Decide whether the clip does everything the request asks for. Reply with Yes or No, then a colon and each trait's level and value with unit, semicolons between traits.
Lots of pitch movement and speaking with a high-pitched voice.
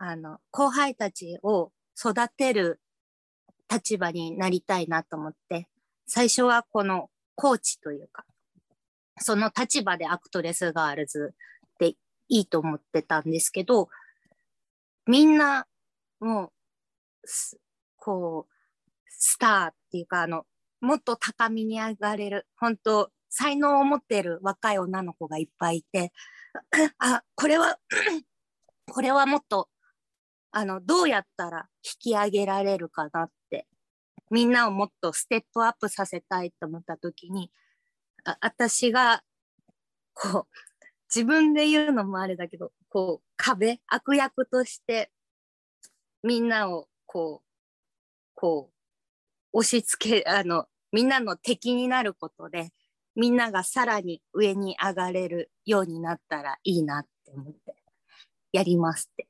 Yes: wide, 6.1 semitones; high, 205 Hz